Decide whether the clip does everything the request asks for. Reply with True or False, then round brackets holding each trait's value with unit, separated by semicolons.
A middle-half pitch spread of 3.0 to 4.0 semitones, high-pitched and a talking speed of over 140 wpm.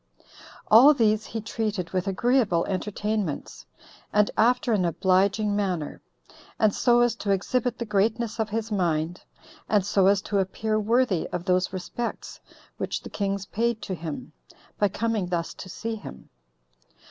True (3.3 semitones; 205 Hz; 150 wpm)